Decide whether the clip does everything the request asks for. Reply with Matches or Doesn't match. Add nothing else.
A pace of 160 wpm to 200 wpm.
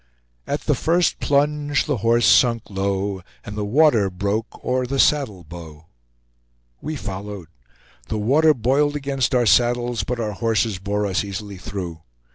Doesn't match